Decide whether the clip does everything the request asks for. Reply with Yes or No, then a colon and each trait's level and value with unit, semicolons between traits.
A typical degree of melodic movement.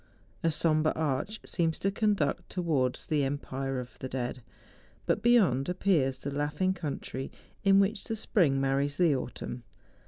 No: wide, 5.7 semitones